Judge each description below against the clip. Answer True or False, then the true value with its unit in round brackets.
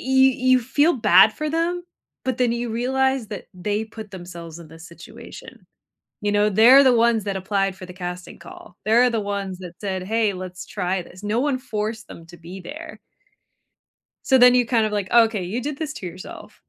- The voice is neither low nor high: False (215 Hz)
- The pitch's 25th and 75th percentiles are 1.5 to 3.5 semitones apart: False (5.1 semitones)